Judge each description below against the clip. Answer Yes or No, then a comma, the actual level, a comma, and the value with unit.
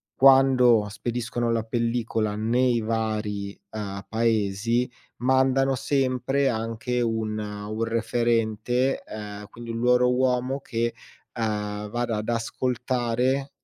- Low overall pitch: Yes, low, 115 Hz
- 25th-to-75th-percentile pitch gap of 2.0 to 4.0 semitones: Yes, narrow, 2.5 semitones